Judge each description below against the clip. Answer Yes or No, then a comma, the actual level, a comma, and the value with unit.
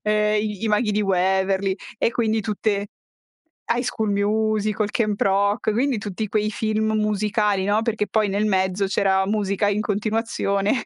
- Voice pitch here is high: Yes, high, 210 Hz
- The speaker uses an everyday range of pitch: No, narrow, 1.4 semitones